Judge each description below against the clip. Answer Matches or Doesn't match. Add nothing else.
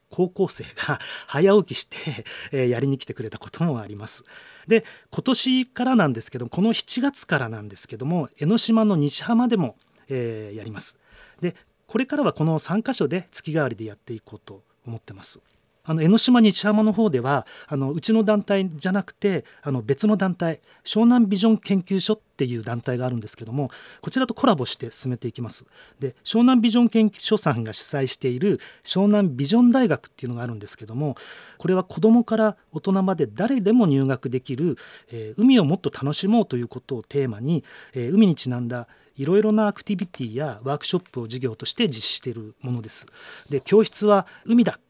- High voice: Doesn't match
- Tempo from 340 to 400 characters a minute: Matches